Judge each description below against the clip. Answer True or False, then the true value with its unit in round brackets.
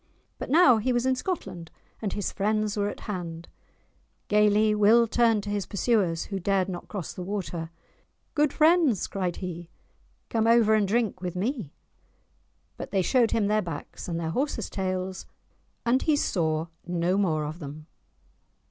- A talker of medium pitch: False (205 Hz)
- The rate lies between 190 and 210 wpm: False (165 wpm)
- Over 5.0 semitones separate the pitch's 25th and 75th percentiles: False (4.3 semitones)